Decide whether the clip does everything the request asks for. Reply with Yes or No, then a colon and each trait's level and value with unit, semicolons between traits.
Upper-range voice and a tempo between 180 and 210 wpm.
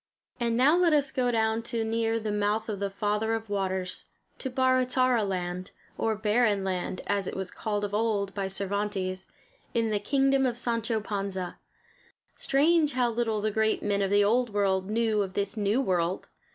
Yes: high, 215 Hz; average, 185 wpm